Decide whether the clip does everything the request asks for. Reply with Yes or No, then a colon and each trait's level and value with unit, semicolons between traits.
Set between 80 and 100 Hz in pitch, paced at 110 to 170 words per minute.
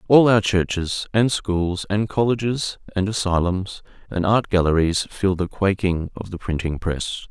Yes: very low, 95 Hz; average, 155 wpm